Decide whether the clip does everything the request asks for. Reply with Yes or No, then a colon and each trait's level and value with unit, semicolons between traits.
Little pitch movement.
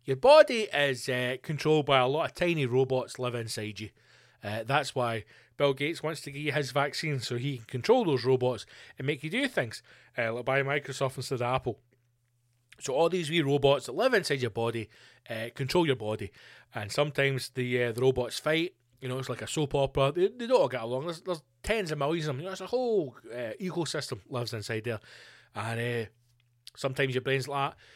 No: average, 3.6 semitones